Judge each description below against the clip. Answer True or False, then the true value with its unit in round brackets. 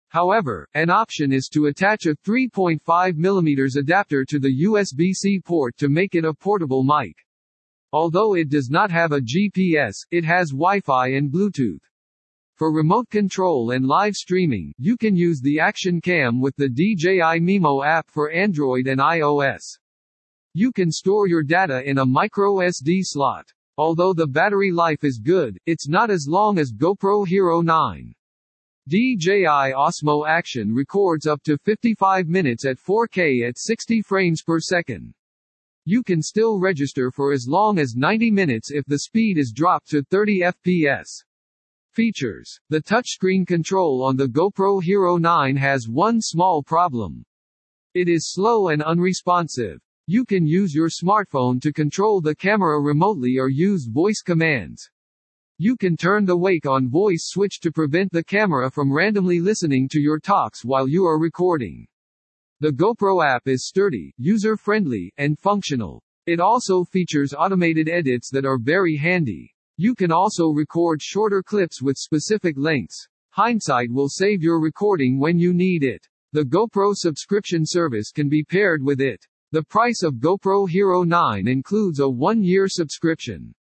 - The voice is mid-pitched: True (165 Hz)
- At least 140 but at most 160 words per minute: True (155 wpm)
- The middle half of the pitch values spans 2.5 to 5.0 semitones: False (5.5 semitones)